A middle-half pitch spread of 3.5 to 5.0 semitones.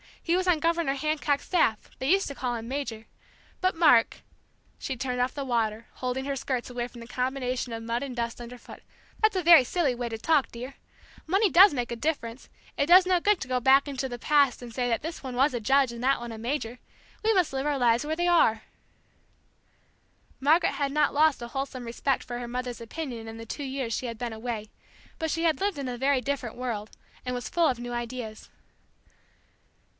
Yes: average, 3.9 semitones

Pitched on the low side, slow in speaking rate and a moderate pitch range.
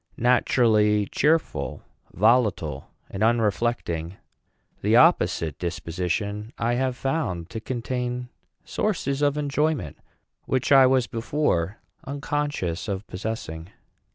No: low, 115 Hz; slow, 100 wpm; wide, 5.8 semitones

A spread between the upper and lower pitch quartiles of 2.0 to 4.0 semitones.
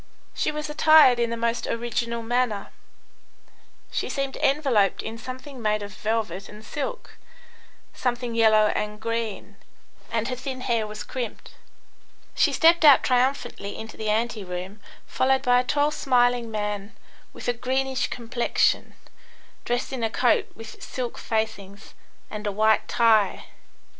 Yes: average, 3.1 semitones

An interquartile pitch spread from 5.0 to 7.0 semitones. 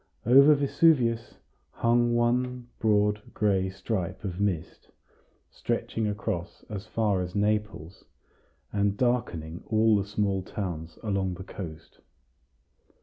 No: average, 3.6 semitones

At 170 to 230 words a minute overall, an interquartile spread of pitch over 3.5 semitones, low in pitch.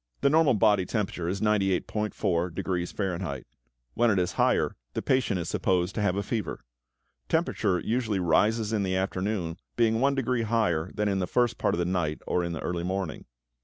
Yes: average, 195 wpm; average, 3.9 semitones; very low, 95 Hz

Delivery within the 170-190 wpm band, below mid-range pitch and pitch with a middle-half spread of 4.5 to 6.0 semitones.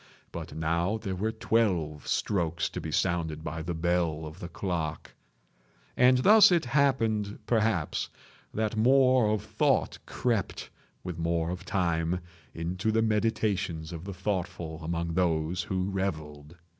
No: average, 140 wpm; very low, 90 Hz; average, 4.8 semitones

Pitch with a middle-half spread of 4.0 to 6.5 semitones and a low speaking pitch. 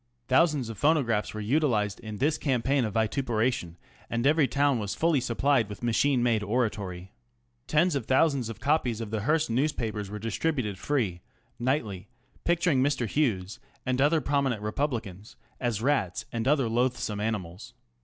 Yes: average, 4.8 semitones; low, 120 Hz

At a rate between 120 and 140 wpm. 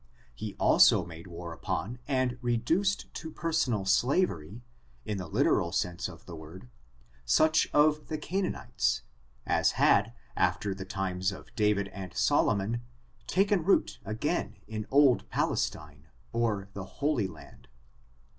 Yes: slow, 135 wpm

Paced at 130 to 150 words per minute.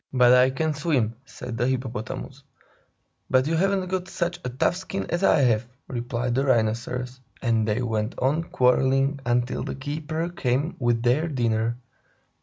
No: average, 160 wpm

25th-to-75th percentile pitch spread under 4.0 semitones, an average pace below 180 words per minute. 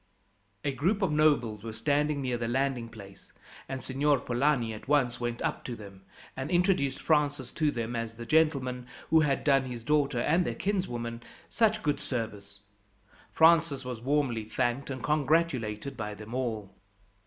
No: average, 4.3 semitones; average, 165 wpm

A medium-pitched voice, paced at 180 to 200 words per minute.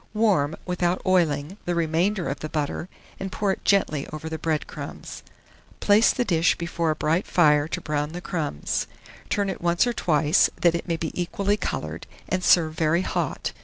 Yes: medium, 170 Hz; average, 185 wpm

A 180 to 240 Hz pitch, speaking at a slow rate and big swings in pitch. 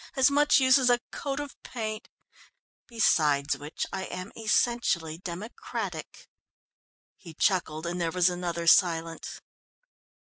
Yes: medium, 185 Hz; slow, 120 wpm; wide, 6.3 semitones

